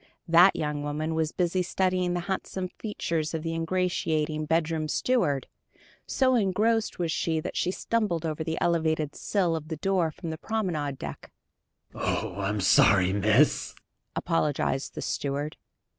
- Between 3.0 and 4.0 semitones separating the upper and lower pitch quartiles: Yes, average, 3.3 semitones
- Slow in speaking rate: No, average, 150 wpm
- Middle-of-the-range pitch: Yes, medium, 160 Hz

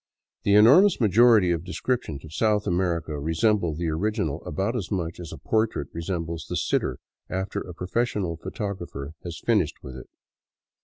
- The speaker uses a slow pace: No, average, 155 wpm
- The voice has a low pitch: Yes, very low, 90 Hz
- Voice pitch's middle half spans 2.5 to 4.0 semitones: No, average, 4.6 semitones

